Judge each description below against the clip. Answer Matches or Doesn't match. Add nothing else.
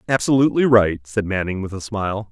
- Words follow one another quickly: Doesn't match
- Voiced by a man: Matches